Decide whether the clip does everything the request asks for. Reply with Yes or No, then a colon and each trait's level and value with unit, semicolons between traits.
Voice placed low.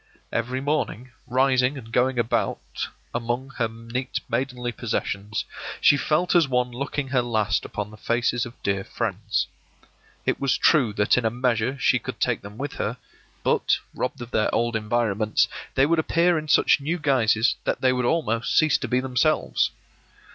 Yes: low, 125 Hz